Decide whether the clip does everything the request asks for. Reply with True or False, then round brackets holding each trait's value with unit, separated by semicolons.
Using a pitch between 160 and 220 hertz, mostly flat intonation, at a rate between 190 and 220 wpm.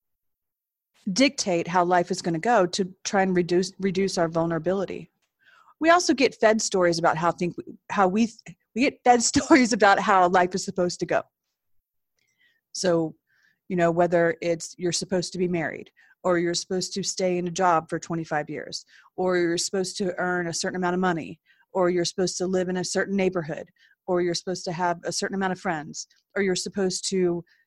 True (185 Hz; 2.2 semitones; 195 wpm)